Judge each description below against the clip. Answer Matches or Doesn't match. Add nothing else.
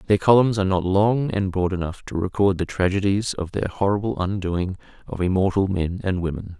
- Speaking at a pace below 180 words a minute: Doesn't match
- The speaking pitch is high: Doesn't match